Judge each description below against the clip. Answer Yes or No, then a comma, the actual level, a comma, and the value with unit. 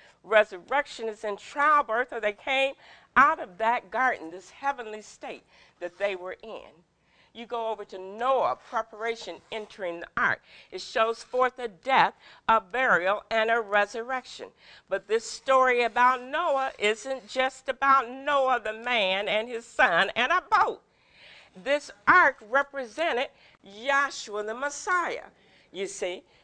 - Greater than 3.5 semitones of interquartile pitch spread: Yes, average, 4.2 semitones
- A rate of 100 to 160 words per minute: Yes, average, 140 wpm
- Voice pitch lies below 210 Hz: No, high, 235 Hz